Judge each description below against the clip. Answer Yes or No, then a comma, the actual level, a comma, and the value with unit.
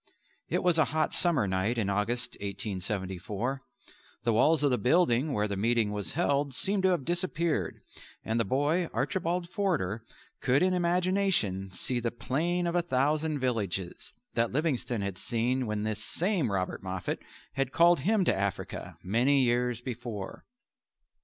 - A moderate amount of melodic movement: No, wide, 7.8 semitones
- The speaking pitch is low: Yes, low, 125 Hz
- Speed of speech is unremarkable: Yes, average, 155 wpm